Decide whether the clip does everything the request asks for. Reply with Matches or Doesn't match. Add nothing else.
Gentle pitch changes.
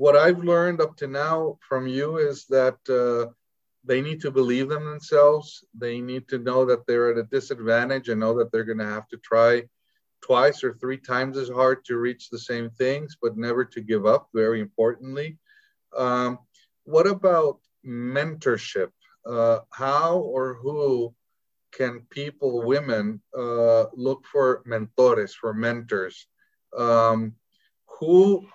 Doesn't match